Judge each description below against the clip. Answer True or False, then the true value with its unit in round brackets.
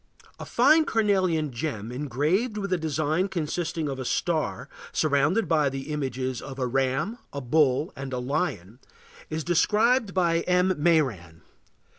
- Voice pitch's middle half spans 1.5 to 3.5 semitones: False (5.3 semitones)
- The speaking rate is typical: True (145 wpm)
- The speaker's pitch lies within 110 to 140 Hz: False (155 Hz)